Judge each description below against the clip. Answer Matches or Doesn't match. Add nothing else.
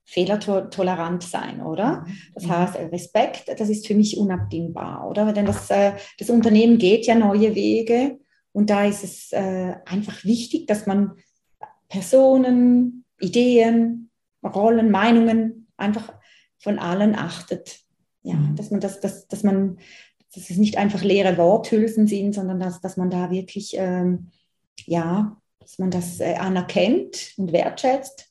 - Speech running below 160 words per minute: Matches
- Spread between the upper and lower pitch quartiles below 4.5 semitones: Matches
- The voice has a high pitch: Matches